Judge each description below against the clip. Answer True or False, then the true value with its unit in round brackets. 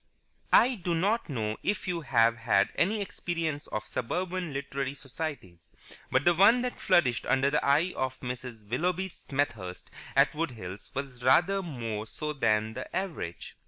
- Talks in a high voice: False (140 Hz)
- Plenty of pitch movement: True (6.9 semitones)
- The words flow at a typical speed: True (160 wpm)